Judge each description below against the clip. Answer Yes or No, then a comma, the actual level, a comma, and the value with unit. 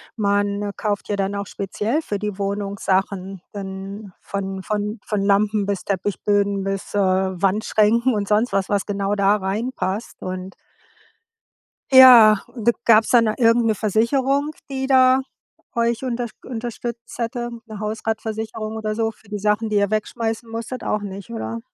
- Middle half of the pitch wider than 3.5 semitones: No, narrow, 2.4 semitones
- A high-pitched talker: Yes, high, 210 Hz